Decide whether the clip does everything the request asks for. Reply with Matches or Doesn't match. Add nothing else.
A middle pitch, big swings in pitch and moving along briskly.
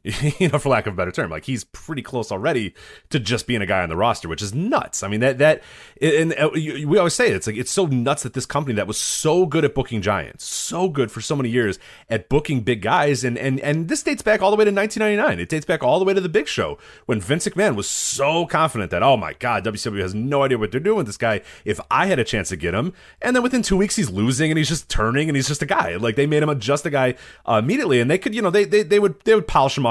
Matches